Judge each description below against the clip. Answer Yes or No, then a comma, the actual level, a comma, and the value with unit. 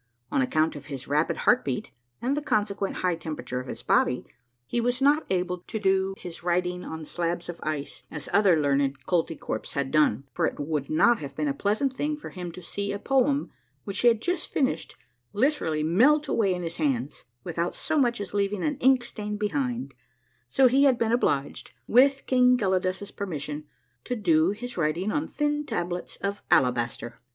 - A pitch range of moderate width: No, wide, 7.9 semitones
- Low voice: No, high, 190 Hz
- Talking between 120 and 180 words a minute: No, average, 190 wpm